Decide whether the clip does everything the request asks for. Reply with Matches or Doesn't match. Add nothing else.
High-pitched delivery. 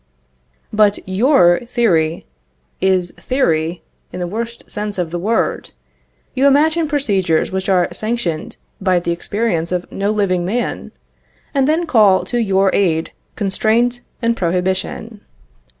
Matches